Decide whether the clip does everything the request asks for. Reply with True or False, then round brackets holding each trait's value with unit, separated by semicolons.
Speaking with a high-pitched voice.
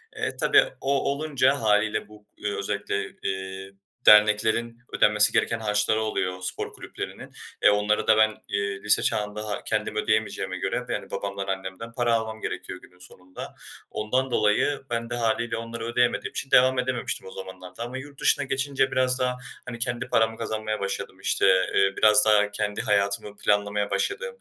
False (110 Hz)